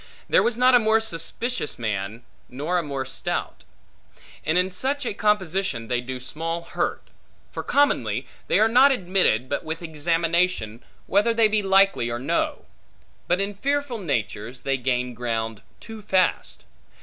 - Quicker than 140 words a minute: Yes, average, 155 wpm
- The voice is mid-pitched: Yes, medium, 170 Hz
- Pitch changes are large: Yes, wide, 8.9 semitones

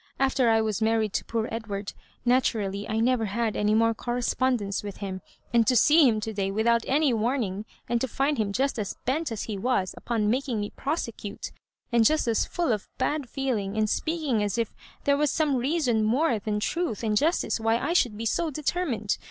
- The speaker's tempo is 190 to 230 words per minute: Yes, average, 200 wpm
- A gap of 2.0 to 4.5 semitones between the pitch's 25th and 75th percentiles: Yes, average, 4.1 semitones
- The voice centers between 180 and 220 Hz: No, high, 230 Hz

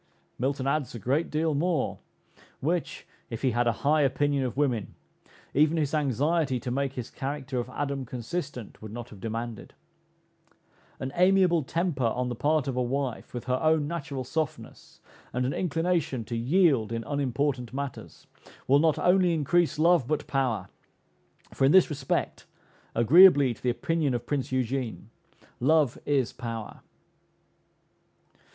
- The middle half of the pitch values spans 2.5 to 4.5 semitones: Yes, average, 4.0 semitones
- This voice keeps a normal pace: Yes, average, 150 wpm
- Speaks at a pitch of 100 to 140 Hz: Yes, low, 135 Hz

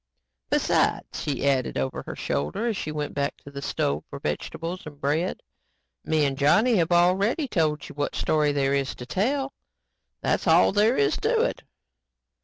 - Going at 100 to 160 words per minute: No, average, 175 wpm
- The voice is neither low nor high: Yes, medium, 155 Hz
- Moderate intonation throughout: No, wide, 6.4 semitones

